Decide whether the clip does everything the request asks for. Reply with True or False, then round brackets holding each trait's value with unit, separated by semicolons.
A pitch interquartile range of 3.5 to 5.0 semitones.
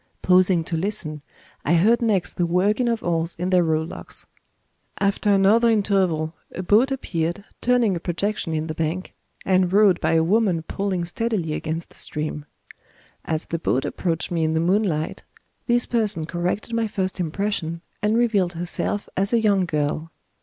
True (4.1 semitones)